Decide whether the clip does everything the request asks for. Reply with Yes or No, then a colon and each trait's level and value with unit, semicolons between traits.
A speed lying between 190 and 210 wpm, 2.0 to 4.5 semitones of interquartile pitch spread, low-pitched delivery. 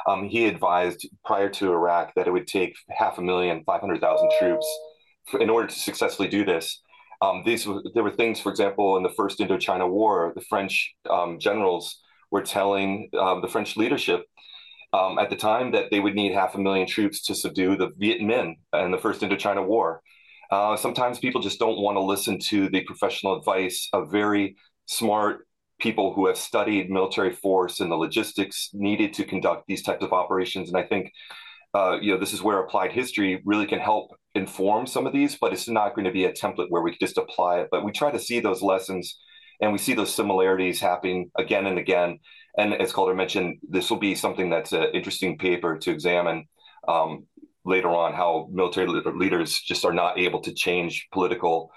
Yes: average, 200 wpm; average, 3.7 semitones; low, 100 Hz